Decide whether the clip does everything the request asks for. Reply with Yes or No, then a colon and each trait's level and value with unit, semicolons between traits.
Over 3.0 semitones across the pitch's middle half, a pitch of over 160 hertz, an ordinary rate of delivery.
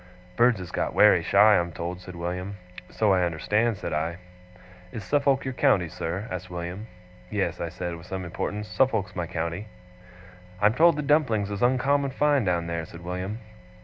No: average, 5.2 semitones; very low, 95 Hz; average, 180 wpm